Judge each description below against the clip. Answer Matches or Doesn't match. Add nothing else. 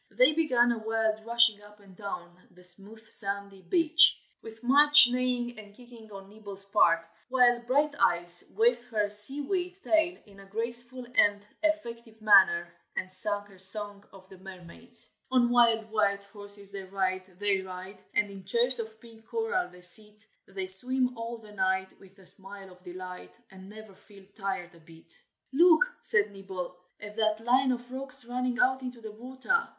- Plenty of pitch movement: Doesn't match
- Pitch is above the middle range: Matches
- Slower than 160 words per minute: Doesn't match